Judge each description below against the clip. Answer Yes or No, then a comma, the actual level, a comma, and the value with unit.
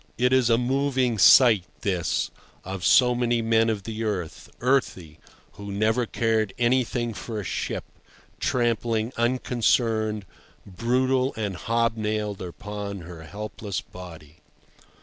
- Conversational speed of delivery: No, slow, 125 wpm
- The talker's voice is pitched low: Yes, low, 110 Hz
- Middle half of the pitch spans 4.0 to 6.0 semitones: No, average, 3.2 semitones